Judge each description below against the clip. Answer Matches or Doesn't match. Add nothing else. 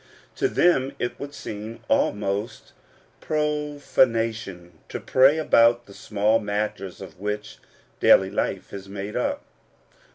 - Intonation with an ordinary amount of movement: Matches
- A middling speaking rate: Doesn't match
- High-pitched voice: Doesn't match